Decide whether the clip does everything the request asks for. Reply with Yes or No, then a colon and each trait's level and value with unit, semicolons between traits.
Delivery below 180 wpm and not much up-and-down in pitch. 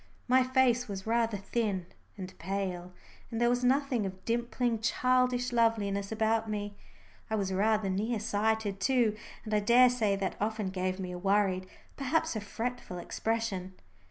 No: average, 155 wpm; average, 3.5 semitones